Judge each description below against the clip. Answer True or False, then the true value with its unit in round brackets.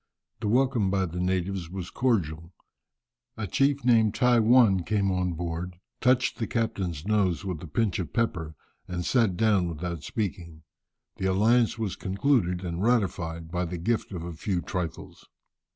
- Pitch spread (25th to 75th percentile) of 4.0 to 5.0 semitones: True (4.5 semitones)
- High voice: False (95 Hz)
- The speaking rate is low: False (160 wpm)